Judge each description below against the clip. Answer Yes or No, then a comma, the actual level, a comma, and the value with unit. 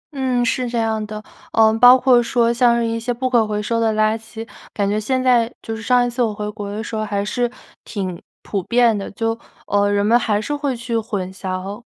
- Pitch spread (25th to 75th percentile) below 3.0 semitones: Yes, narrow, 2.5 semitones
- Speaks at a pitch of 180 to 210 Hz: No, high, 225 Hz